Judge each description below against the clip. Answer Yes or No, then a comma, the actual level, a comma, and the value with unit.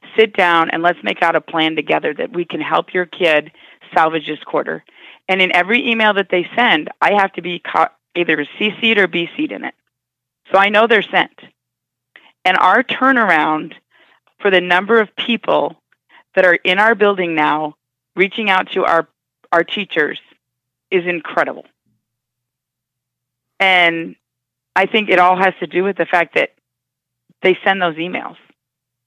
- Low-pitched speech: No, medium, 175 Hz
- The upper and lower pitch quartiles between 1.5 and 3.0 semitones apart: No, average, 4.8 semitones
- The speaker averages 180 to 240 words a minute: No, average, 165 wpm